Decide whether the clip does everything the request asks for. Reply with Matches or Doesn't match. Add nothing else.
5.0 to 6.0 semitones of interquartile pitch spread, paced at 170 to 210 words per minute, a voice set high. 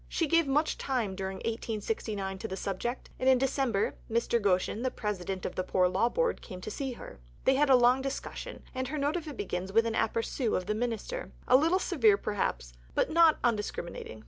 Matches